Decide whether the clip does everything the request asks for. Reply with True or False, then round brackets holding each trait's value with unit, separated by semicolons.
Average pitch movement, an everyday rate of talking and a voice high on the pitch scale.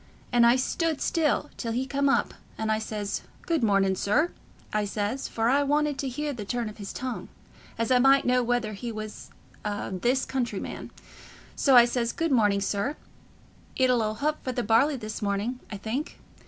True (4.1 semitones; 195 wpm; 240 Hz)